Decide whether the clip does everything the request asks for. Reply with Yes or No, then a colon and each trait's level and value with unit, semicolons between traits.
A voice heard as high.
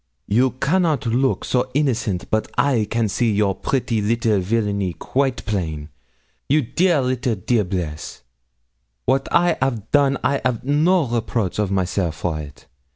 No: low, 115 Hz